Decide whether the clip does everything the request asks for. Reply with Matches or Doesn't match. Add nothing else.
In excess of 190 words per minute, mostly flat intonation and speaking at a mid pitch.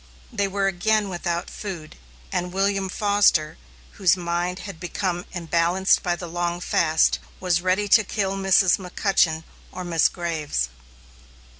Doesn't match